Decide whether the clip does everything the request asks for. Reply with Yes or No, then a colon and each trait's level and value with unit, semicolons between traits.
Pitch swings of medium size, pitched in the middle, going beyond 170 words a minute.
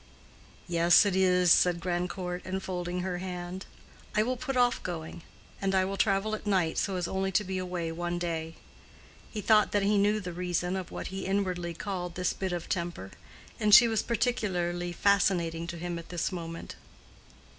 No: narrow, 2.2 semitones; medium, 180 Hz; average, 180 wpm